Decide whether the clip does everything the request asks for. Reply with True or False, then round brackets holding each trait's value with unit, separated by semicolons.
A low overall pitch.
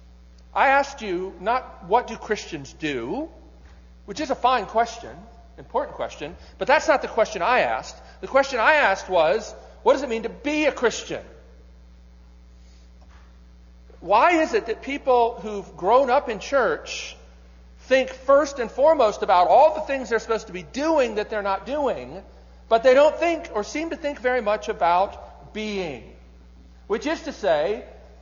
False (215 Hz)